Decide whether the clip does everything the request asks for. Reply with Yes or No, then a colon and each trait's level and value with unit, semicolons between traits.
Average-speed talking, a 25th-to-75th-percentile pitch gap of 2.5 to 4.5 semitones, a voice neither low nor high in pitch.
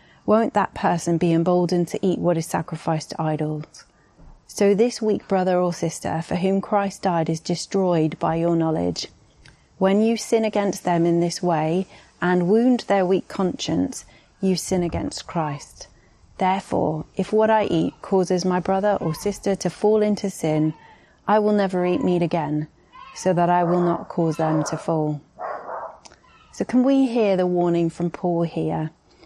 Yes: average, 170 wpm; average, 3.3 semitones; medium, 180 Hz